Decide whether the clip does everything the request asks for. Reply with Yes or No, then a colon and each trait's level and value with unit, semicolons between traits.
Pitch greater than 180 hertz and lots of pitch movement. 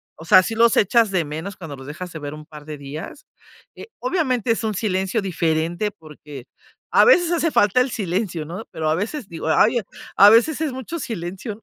Yes: high, 190 Hz; wide, 6.4 semitones